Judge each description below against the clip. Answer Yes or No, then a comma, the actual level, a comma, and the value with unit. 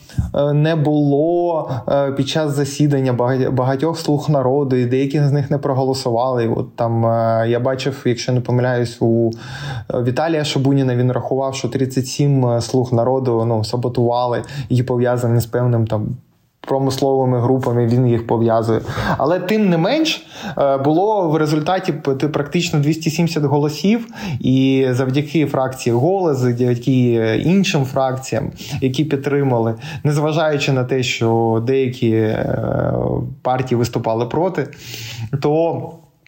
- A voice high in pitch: No, low, 135 Hz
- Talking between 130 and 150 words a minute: No, average, 115 wpm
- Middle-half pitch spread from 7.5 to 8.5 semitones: No, average, 3.5 semitones